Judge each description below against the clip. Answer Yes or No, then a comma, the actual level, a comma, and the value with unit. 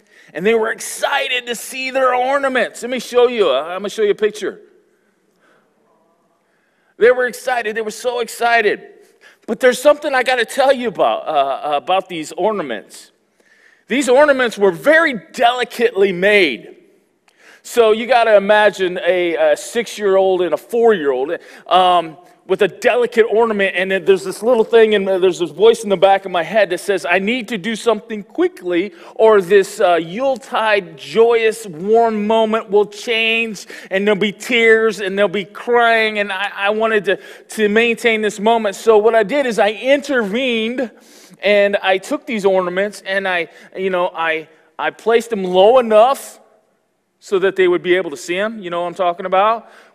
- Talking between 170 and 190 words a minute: Yes, average, 180 wpm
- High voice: Yes, high, 220 Hz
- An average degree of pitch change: Yes, average, 4.1 semitones